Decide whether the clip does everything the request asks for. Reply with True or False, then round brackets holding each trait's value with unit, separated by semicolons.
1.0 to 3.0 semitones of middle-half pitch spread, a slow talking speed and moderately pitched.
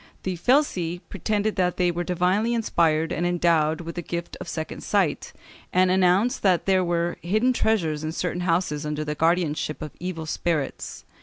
False (2.5 semitones; 170 wpm; 175 Hz)